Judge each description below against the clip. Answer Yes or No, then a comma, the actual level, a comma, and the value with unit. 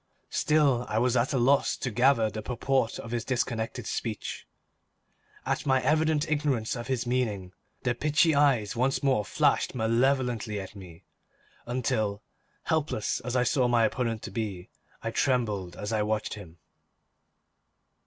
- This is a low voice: Yes, low, 120 Hz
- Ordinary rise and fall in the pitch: Yes, average, 3.6 semitones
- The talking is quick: No, average, 150 wpm